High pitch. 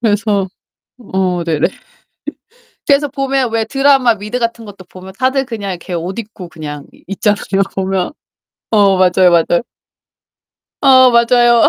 Yes: high, 210 Hz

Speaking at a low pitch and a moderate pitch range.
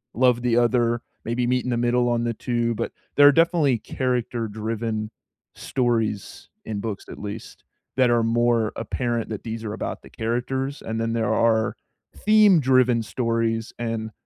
No: low, 115 Hz; narrow, 1.7 semitones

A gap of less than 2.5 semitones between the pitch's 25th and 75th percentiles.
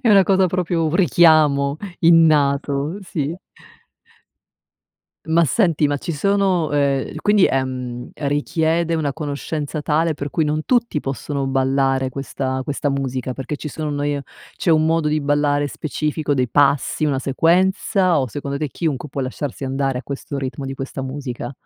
No: average, 2.9 semitones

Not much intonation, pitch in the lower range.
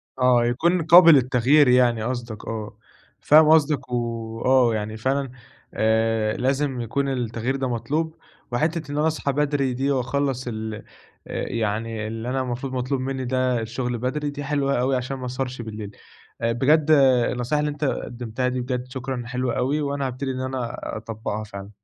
No: average, 3.0 semitones; low, 125 Hz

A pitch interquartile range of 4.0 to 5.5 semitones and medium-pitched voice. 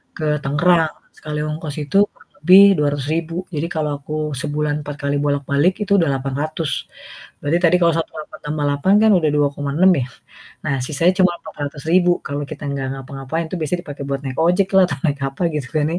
No: average, 2.9 semitones; medium, 150 Hz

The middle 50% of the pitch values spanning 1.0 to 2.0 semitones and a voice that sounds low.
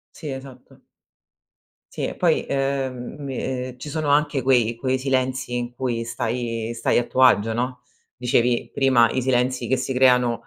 Yes: narrow, 1.7 semitones; low, 125 Hz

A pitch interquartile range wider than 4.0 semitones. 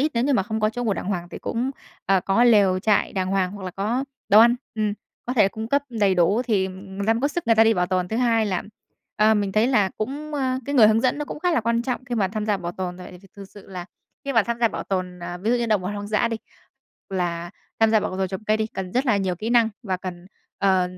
No: average, 3.7 semitones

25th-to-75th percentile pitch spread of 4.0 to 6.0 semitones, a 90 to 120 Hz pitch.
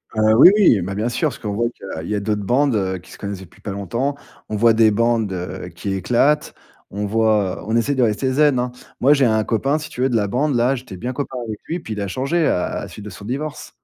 Yes: average, 4.5 semitones; low, 115 Hz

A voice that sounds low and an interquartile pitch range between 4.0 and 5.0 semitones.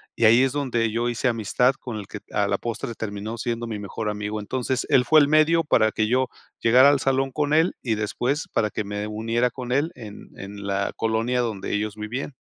No: low, 115 Hz; average, 3.4 semitones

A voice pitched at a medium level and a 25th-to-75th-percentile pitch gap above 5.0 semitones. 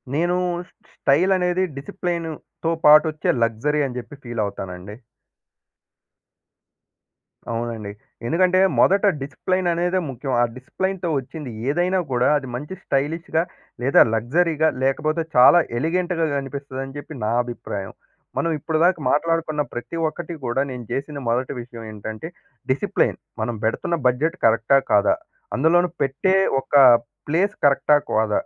Yes: medium, 145 Hz; wide, 5.5 semitones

